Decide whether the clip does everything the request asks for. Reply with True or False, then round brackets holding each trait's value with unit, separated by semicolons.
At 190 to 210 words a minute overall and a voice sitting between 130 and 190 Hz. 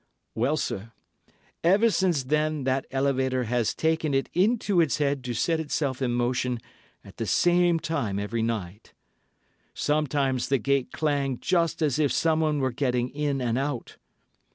False (155 wpm; 140 Hz)